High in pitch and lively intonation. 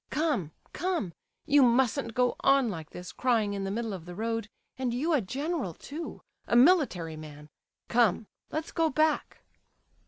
Yes: high, 235 Hz; wide, 7.0 semitones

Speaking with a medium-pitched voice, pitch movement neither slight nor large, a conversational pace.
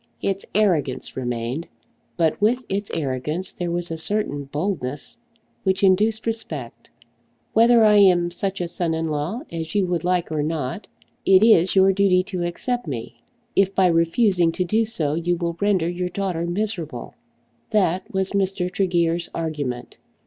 Yes: medium, 175 Hz; average, 3.4 semitones; average, 155 wpm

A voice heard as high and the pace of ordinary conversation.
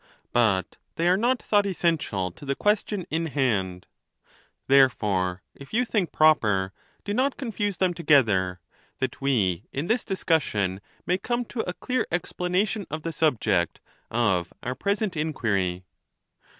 No: medium, 150 Hz; average, 150 wpm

